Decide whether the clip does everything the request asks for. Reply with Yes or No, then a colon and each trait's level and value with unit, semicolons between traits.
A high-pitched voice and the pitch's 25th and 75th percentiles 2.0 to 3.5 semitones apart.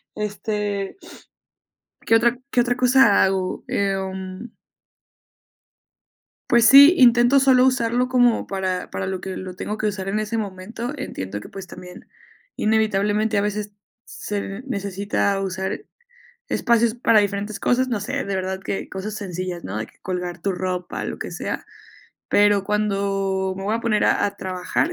Yes: high, 205 Hz; average, 3.2 semitones